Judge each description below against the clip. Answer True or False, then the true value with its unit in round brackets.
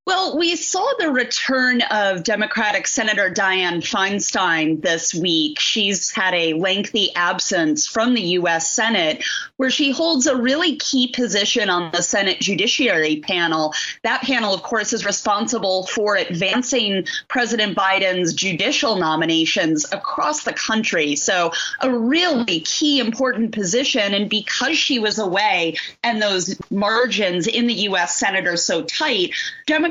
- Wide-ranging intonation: True (5.8 semitones)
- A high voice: True (215 Hz)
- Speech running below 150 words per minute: True (140 wpm)